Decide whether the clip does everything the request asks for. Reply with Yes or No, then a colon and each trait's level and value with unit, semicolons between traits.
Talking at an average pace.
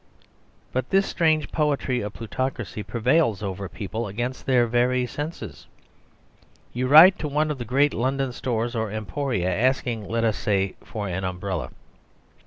Yes: average, 150 wpm